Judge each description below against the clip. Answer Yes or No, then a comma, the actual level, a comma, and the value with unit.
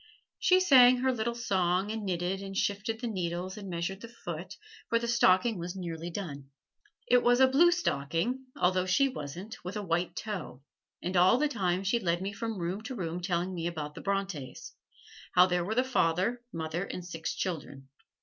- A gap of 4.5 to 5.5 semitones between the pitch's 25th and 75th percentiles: Yes, average, 5.0 semitones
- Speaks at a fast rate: No, average, 190 wpm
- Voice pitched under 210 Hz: Yes, high, 190 Hz